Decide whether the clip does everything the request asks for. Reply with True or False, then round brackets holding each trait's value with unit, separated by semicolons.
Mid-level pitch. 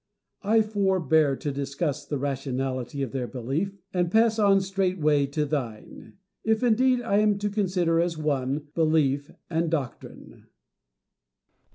True (160 Hz)